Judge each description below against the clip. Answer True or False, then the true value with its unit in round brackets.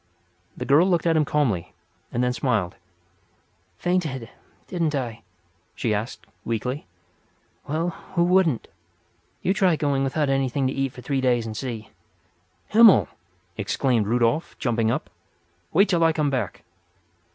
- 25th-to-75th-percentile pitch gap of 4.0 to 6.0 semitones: True (5.5 semitones)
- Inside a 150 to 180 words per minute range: False (140 wpm)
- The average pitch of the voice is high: False (135 Hz)